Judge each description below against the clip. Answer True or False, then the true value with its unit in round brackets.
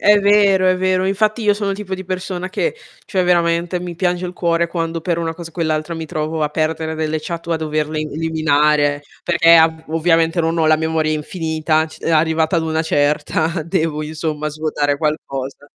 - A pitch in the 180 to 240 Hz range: False (160 Hz)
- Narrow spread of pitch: True (2.3 semitones)